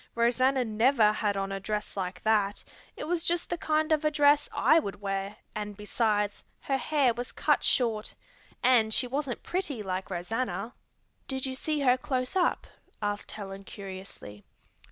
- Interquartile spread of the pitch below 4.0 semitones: No, average, 5.1 semitones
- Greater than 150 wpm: Yes, average, 165 wpm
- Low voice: No, high, 230 Hz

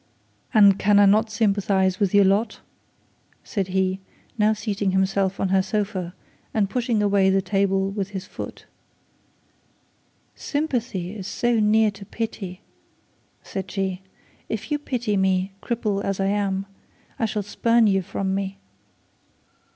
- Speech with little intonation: Yes, narrow, 2.0 semitones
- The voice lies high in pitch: Yes, high, 200 Hz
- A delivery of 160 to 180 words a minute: No, average, 140 wpm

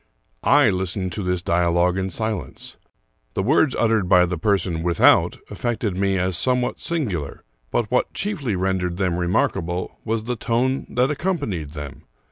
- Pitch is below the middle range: Yes, very low, 95 Hz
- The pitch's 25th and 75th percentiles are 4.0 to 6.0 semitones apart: Yes, average, 5.1 semitones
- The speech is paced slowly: No, average, 155 wpm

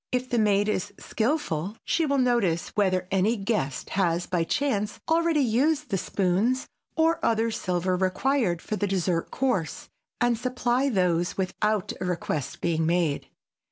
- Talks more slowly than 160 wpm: Yes, average, 150 wpm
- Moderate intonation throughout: No, wide, 5.8 semitones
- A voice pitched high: Yes, high, 205 Hz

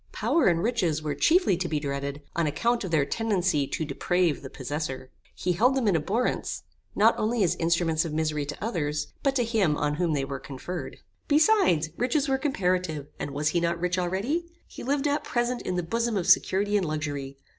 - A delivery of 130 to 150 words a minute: No, average, 200 wpm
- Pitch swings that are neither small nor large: No, wide, 7.3 semitones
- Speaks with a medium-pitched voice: Yes, medium, 175 Hz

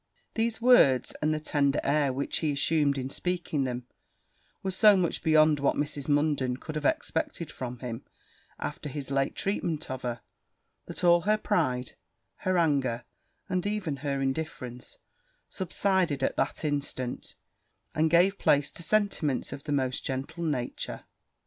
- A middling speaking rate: Yes, average, 150 wpm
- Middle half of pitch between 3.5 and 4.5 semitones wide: Yes, average, 4.2 semitones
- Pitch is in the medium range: Yes, medium, 150 Hz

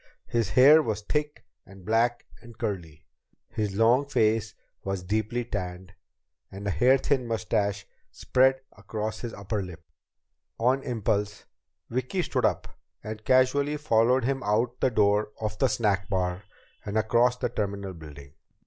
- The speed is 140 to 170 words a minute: Yes, average, 145 wpm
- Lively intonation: No, average, 3.7 semitones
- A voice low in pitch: Yes, low, 110 Hz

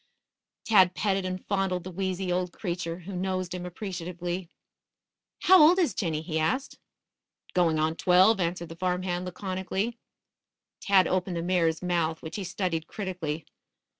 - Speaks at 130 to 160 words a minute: Yes, average, 150 wpm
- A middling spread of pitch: No, narrow, 1.9 semitones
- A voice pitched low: No, medium, 180 Hz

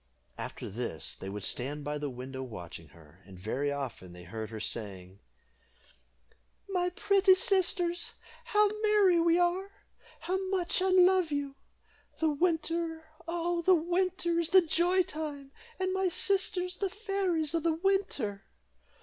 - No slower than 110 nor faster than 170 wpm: Yes, average, 145 wpm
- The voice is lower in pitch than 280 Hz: No, very high, 335 Hz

